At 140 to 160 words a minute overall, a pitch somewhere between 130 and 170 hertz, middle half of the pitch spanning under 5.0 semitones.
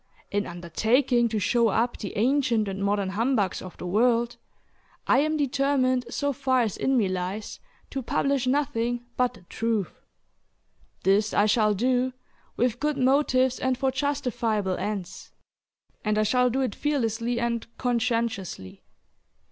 No: average, 145 wpm; high, 235 Hz; average, 3.7 semitones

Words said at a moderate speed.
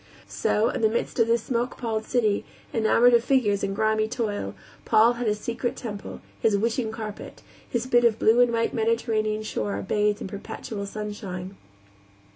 Yes: average, 170 wpm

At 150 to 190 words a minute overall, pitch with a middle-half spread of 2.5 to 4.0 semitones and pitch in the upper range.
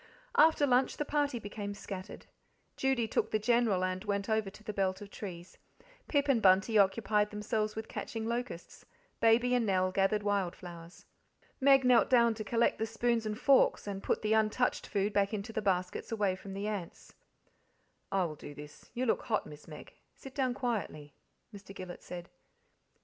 Yes: average, 180 wpm; average, 3.4 semitones; high, 210 Hz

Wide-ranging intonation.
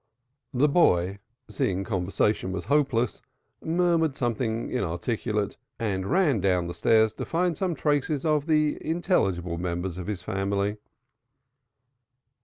Yes: wide, 7.9 semitones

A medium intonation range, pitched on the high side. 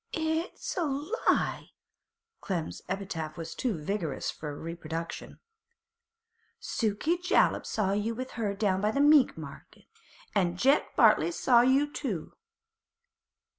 No: wide, 8.3 semitones; high, 210 Hz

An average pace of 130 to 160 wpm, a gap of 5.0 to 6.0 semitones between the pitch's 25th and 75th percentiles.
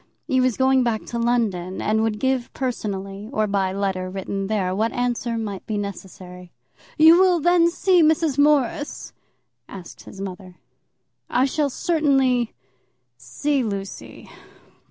Yes: slow, 135 wpm; wide, 5.6 semitones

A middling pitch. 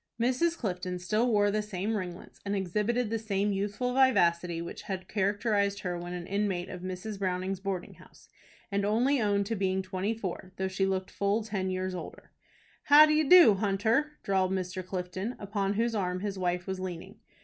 No: high, 195 Hz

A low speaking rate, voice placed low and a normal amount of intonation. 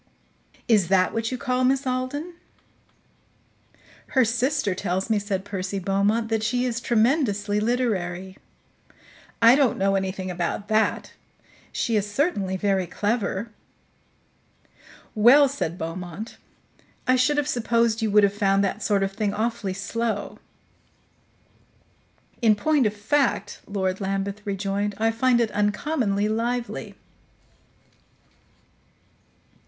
No: slow, 120 wpm; high, 210 Hz; average, 3.5 semitones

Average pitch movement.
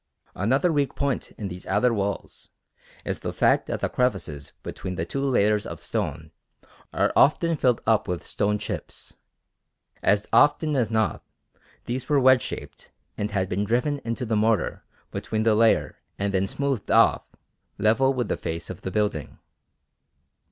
Yes: average, 4.7 semitones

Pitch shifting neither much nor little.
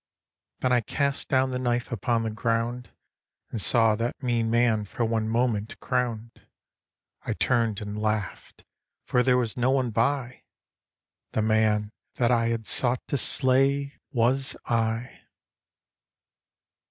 No: narrow, 2.2 semitones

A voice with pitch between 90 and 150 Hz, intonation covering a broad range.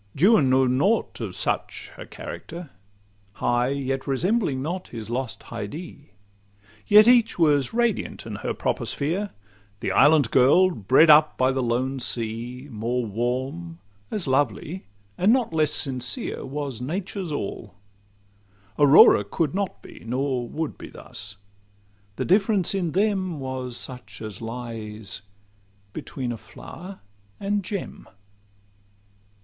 Yes: low, 135 Hz; wide, 6.7 semitones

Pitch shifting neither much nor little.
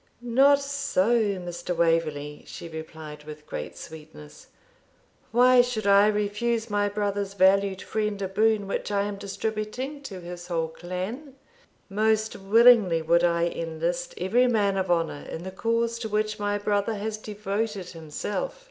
Yes: average, 4.2 semitones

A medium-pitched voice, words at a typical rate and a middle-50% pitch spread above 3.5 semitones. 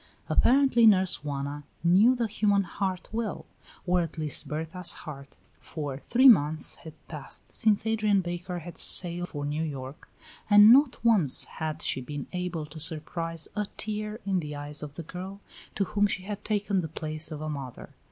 Yes: medium, 175 Hz; average, 175 wpm; average, 5.3 semitones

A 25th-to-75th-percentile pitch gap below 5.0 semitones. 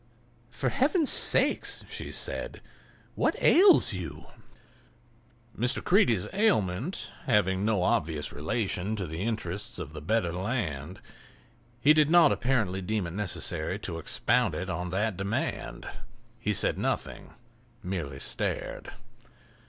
No: wide, 5.4 semitones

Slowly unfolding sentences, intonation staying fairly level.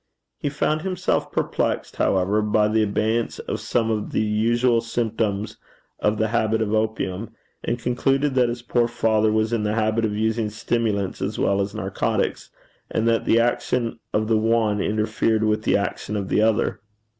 No: average, 175 wpm; narrow, 1.6 semitones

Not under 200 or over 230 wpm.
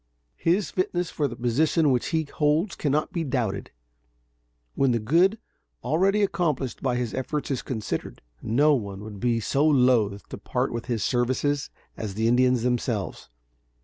No: average, 155 wpm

